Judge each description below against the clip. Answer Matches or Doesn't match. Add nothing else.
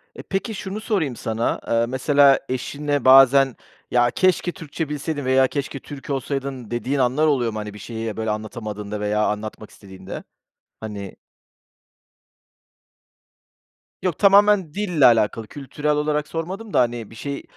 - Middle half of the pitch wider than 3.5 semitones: Matches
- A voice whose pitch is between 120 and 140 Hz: Matches